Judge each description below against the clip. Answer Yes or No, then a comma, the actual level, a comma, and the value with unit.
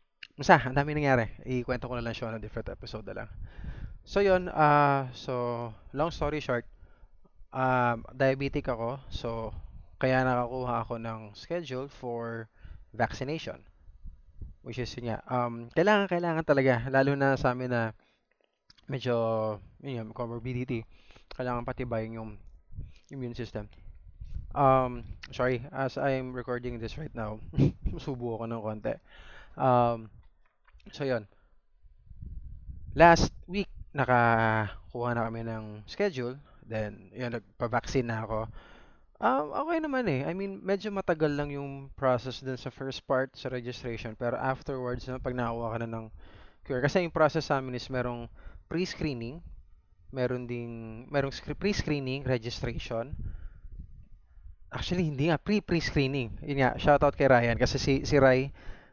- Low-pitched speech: Yes, low, 125 Hz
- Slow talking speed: No, average, 140 wpm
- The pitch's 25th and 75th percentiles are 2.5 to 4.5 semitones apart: Yes, average, 3.7 semitones